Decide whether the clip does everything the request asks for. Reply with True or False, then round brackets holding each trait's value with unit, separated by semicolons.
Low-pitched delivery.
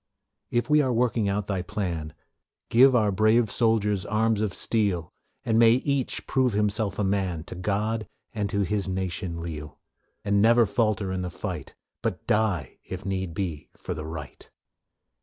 True (100 Hz)